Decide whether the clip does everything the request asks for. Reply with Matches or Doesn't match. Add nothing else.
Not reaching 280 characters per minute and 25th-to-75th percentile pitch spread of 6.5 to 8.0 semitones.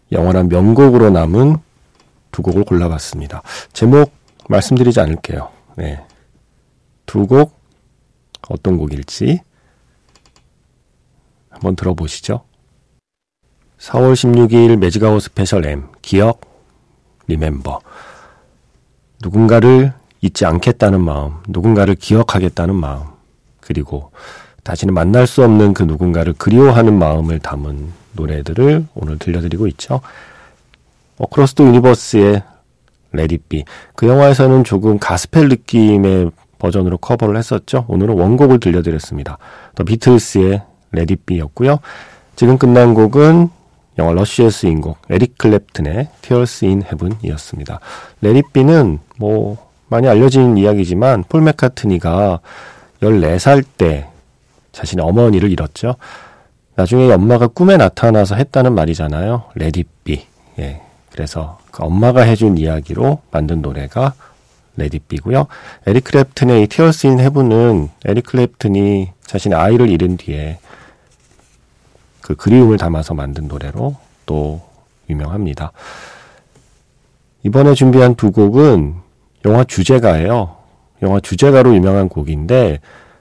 Matches